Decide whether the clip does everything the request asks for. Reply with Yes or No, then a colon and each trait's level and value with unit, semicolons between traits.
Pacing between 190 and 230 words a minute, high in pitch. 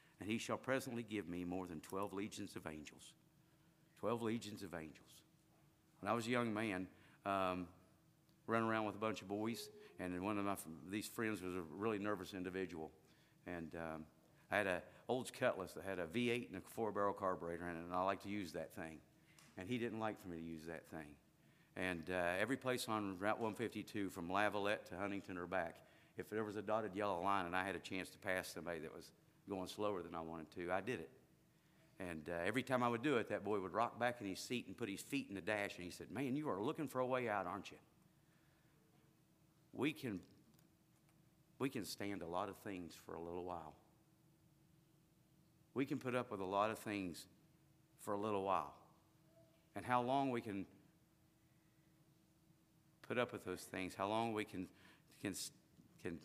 No: fast, 205 wpm; low, 105 Hz